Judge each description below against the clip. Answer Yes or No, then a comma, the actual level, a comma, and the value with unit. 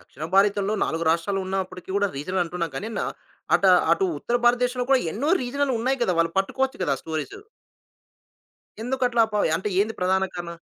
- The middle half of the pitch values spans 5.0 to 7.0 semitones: Yes, wide, 5.6 semitones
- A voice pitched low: No, high, 200 Hz